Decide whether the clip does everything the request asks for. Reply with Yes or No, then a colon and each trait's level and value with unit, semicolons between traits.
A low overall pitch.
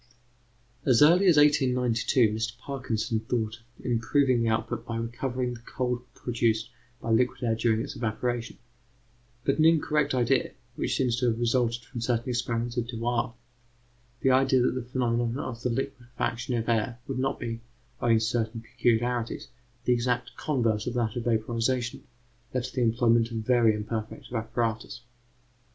Yes: low, 120 Hz